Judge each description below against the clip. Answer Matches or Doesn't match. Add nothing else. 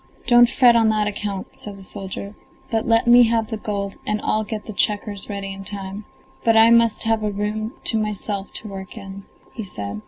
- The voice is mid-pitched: Doesn't match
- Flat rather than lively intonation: Matches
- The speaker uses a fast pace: Matches